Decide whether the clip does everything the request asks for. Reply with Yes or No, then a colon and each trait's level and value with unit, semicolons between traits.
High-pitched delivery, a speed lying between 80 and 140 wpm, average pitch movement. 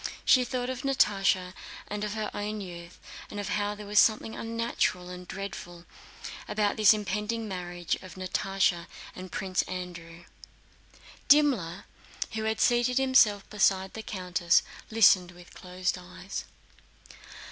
Yes: high, 195 Hz; slow, 135 wpm; average, 3.2 semitones